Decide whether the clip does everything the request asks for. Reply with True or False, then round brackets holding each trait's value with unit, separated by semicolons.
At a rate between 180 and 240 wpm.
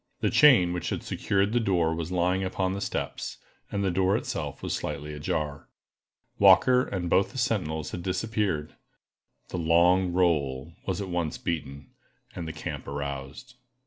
False (160 wpm)